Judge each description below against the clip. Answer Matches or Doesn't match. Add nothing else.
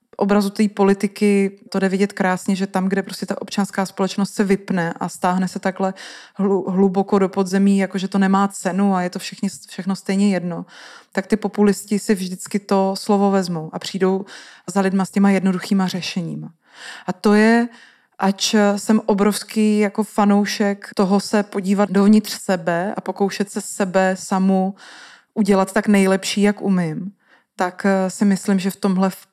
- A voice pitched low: Doesn't match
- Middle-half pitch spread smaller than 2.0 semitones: Matches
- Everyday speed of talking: Matches